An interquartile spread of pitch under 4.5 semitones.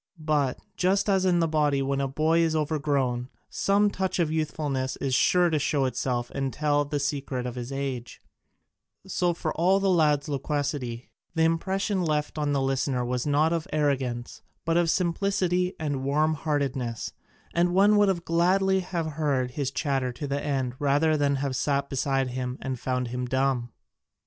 Yes: average, 3.8 semitones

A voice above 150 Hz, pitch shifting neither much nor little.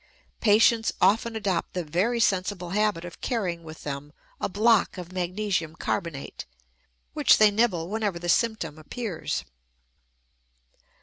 Yes: medium, 185 Hz; average, 4.2 semitones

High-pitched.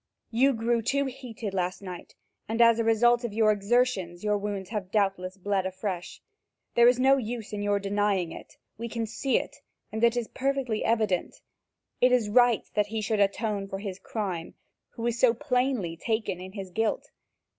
Yes: high, 215 Hz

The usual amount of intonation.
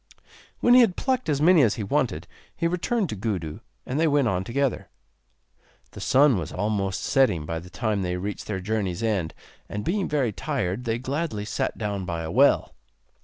No: wide, 7.4 semitones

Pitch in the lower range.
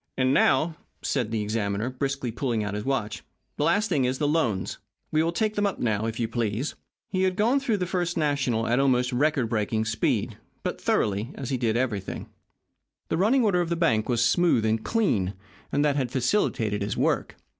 Yes: low, 130 Hz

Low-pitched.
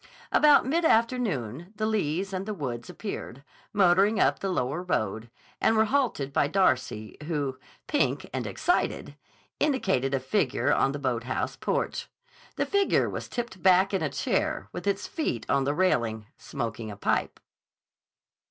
No: medium, 175 Hz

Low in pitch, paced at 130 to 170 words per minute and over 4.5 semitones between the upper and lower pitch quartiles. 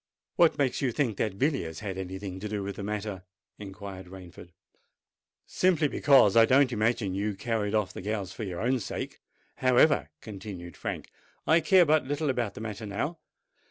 No: low, 105 Hz; average, 180 wpm; average, 5.2 semitones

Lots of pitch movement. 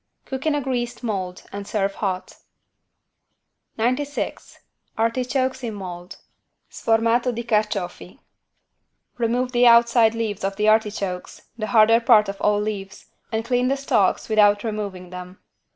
No: average, 3.2 semitones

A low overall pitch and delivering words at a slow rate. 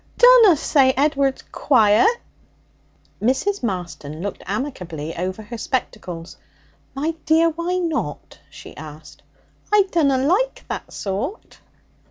No: very high, 260 Hz; slow, 110 wpm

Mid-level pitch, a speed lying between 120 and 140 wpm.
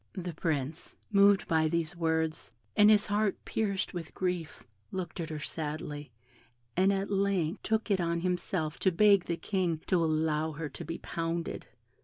No: medium, 170 Hz; average, 165 wpm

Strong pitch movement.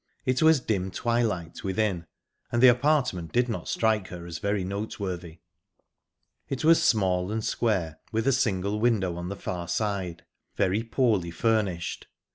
No: average, 4.5 semitones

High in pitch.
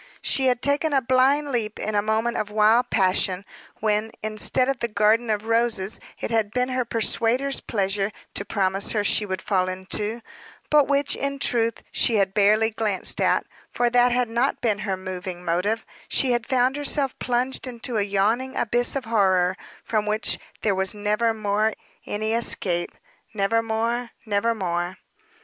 Yes: high, 220 Hz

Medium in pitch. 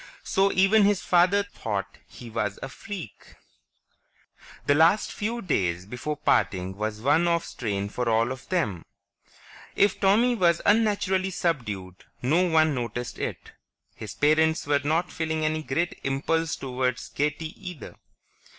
Yes: medium, 155 Hz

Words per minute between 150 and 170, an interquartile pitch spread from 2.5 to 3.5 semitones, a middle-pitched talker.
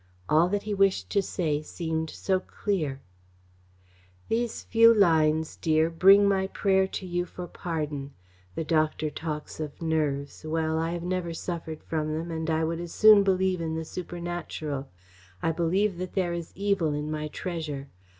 Yes: average, 160 wpm; average, 3.1 semitones; medium, 165 Hz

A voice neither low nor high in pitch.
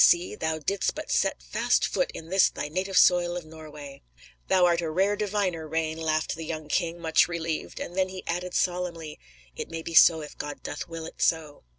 Yes: medium, 165 Hz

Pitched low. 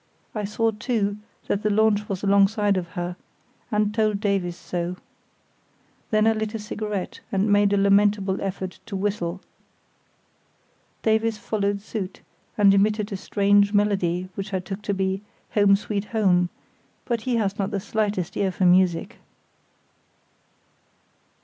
No: high, 200 Hz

